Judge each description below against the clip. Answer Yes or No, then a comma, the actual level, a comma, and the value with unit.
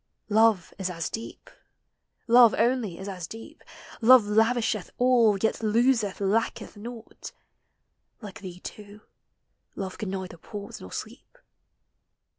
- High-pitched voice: Yes, high, 215 Hz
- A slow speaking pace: Yes, slow, 120 wpm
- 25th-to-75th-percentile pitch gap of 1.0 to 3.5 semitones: Yes, average, 3.0 semitones